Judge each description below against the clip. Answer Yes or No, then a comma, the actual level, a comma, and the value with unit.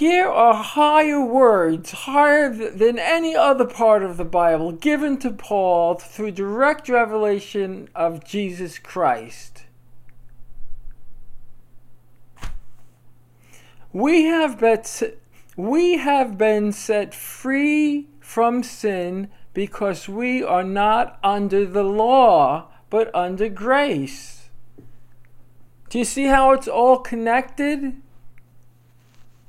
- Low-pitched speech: No, high, 200 Hz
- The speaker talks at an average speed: No, slow, 90 wpm